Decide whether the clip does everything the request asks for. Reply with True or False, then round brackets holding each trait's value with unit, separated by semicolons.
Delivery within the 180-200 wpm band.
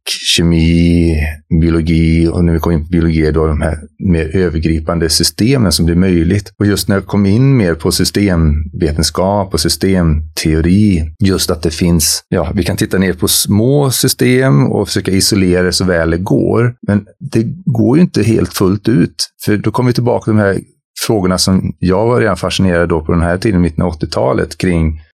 True (190 wpm)